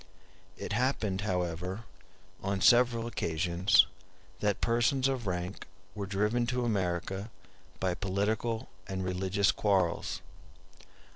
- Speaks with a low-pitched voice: Yes, low, 100 Hz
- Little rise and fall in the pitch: No, average, 3.9 semitones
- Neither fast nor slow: No, slow, 100 wpm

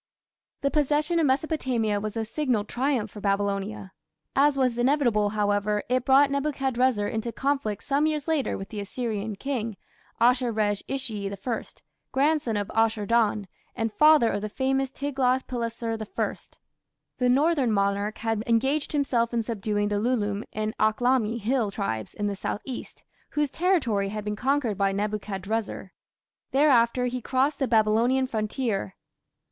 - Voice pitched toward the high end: Yes, high, 230 Hz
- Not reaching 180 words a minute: Yes, average, 150 wpm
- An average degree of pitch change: Yes, average, 4.3 semitones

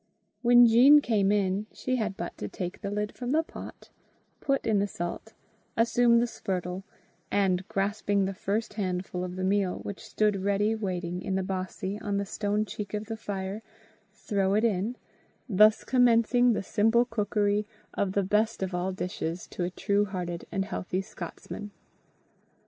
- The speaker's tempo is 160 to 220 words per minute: Yes, average, 170 wpm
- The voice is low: No, high, 205 Hz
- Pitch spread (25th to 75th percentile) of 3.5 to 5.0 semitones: No, average, 2.7 semitones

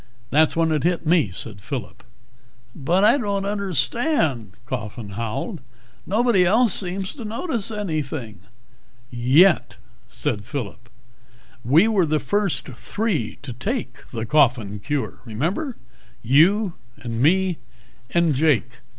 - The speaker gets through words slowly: Yes, slow, 125 wpm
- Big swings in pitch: Yes, wide, 8.5 semitones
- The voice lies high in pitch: No, medium, 155 Hz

